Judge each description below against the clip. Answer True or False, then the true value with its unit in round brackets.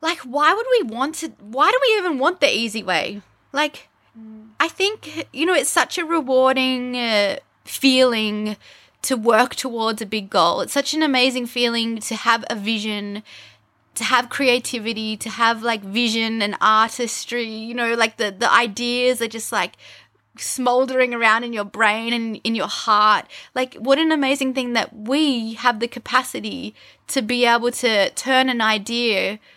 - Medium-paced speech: True (170 wpm)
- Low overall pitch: False (240 Hz)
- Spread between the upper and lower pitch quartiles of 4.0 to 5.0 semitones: False (3.0 semitones)